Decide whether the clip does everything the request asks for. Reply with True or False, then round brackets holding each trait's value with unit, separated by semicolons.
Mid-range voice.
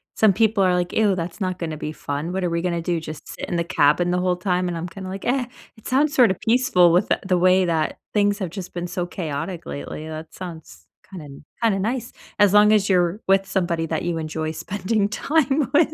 True (180 Hz)